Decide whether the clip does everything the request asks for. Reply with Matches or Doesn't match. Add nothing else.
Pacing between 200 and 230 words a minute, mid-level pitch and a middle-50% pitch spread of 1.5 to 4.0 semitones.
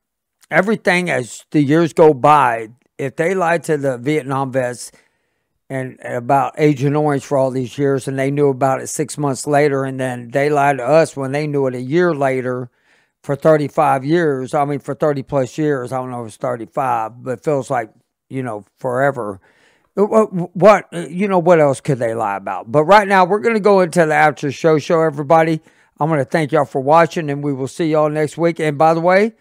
Matches